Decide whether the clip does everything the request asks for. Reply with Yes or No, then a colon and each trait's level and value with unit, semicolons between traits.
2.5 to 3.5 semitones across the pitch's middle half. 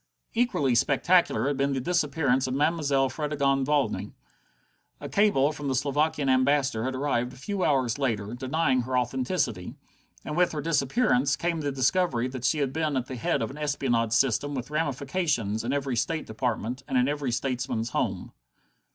Yes: average, 3.0 semitones